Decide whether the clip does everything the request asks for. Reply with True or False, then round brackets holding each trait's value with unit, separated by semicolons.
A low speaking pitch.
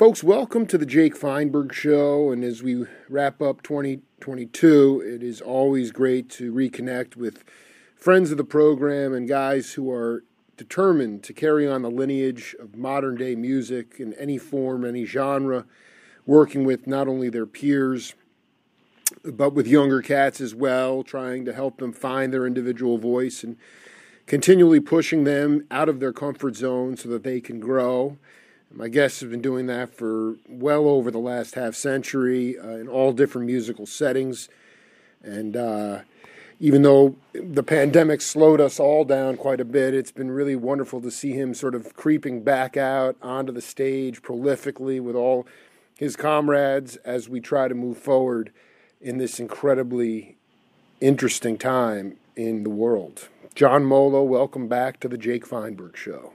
True (130 Hz)